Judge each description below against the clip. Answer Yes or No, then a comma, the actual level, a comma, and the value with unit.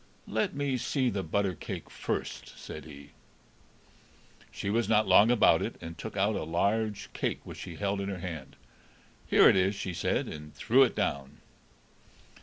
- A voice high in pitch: No, low, 100 Hz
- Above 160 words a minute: Yes, average, 175 wpm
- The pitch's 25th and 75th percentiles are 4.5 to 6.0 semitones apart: Yes, average, 5.0 semitones